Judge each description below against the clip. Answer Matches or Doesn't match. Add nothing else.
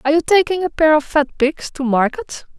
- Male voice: Doesn't match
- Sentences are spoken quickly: Matches